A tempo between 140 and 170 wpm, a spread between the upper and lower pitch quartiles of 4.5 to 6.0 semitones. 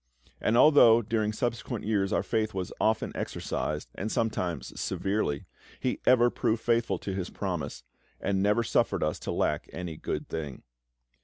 No: average, 155 wpm; average, 3.4 semitones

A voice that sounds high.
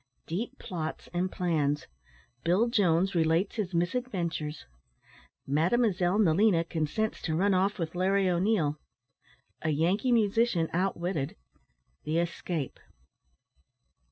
No: medium, 175 Hz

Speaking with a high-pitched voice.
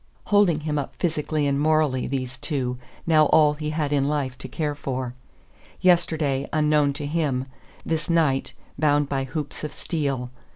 No: medium, 150 Hz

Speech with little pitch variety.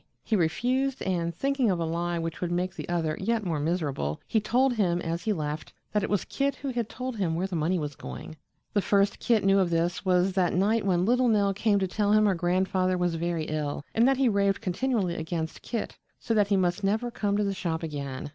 No: average, 4.1 semitones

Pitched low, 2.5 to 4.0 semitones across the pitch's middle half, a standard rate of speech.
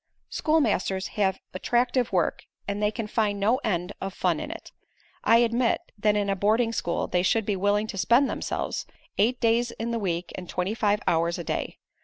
No: high, 210 Hz; average, 3.4 semitones; average, 195 wpm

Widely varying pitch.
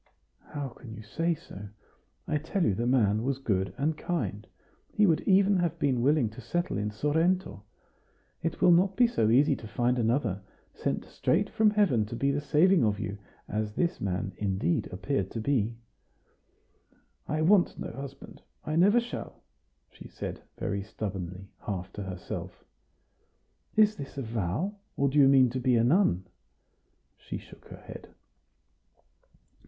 Yes: wide, 7.7 semitones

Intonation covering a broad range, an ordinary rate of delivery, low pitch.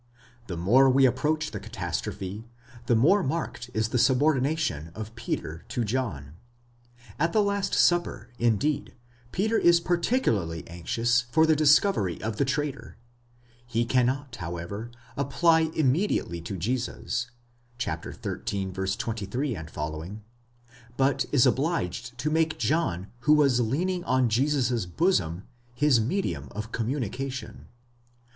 No: wide, 6.2 semitones; slow, 120 wpm; low, 125 Hz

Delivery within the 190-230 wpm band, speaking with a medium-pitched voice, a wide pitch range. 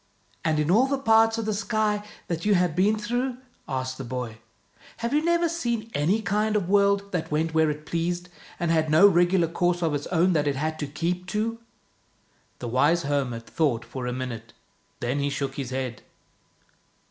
Yes: average, 200 wpm; medium, 170 Hz; wide, 6.6 semitones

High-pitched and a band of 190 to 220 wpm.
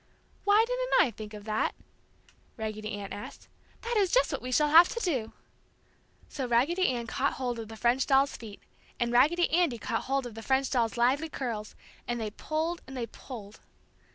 Yes: very high, 250 Hz; average, 195 wpm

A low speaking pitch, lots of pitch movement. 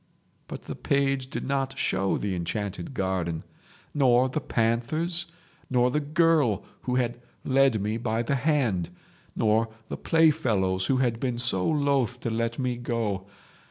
No: low, 120 Hz; average, 4.1 semitones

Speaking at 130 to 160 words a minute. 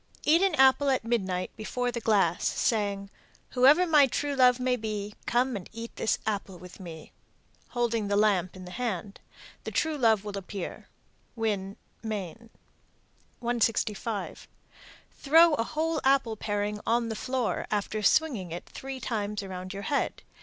Yes: average, 155 wpm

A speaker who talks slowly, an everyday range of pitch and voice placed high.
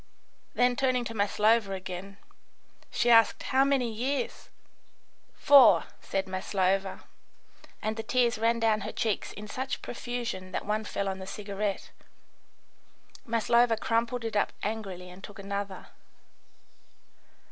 Yes: slow, 125 wpm; average, 3.2 semitones; high, 215 Hz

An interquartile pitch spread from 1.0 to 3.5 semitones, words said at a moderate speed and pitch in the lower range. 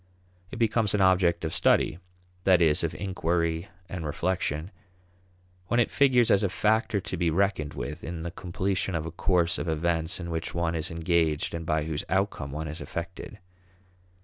Yes: average, 2.9 semitones; average, 175 wpm; very low, 85 Hz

